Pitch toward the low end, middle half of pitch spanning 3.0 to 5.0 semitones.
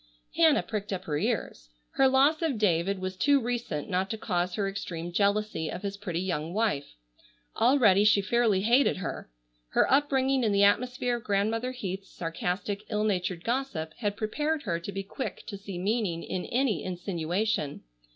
No: high, 200 Hz; average, 4.7 semitones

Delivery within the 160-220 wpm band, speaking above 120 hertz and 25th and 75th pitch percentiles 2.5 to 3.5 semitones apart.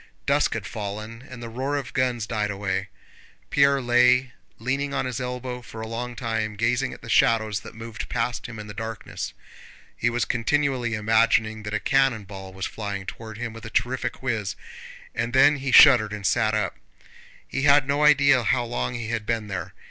No: average, 195 wpm; low, 115 Hz; average, 2.9 semitones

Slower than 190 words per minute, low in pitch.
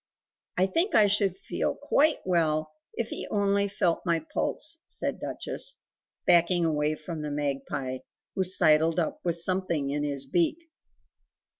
No: average, 145 wpm; medium, 170 Hz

